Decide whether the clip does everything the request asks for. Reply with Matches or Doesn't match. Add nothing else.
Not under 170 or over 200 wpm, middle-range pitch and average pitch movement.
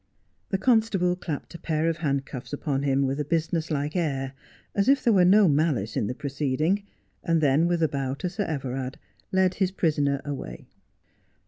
Matches